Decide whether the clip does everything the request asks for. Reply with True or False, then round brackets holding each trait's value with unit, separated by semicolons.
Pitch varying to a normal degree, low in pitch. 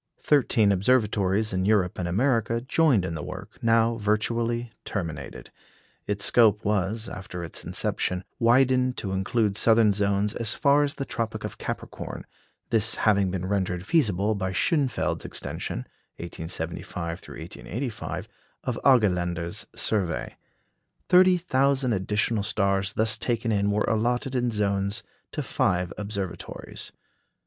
True (3.6 semitones; 105 Hz)